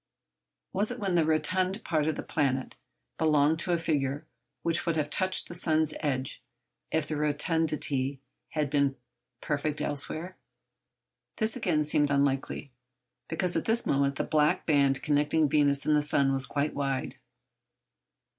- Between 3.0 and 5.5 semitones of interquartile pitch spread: No, narrow, 2.4 semitones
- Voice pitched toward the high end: No, medium, 150 Hz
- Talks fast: No, average, 150 wpm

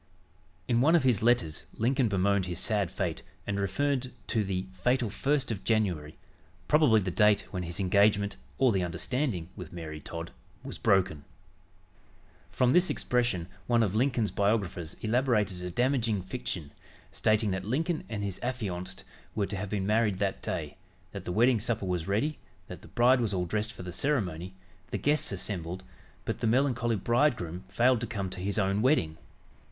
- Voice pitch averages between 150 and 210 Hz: No, low, 105 Hz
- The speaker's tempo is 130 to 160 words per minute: No, average, 170 wpm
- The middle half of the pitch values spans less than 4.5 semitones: No, average, 4.8 semitones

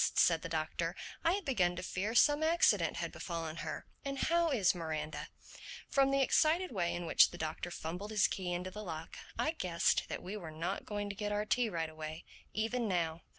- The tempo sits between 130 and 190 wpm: No, fast, 205 wpm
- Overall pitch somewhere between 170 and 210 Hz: Yes, medium, 185 Hz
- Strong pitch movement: Yes, wide, 6.2 semitones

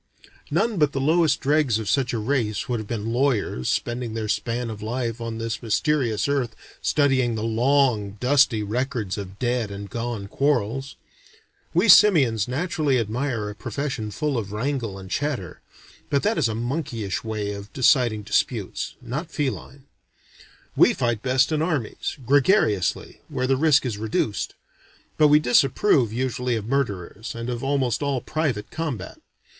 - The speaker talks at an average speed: Yes, average, 155 wpm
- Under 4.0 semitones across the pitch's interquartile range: No, average, 4.3 semitones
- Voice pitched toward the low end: Yes, low, 125 Hz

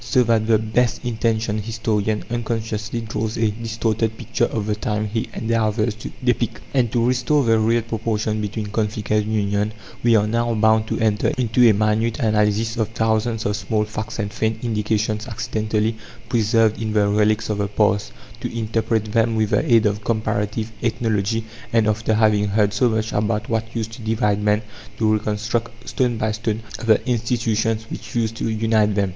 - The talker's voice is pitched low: Yes, low, 110 Hz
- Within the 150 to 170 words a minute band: No, average, 180 wpm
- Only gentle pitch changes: Yes, narrow, 1.2 semitones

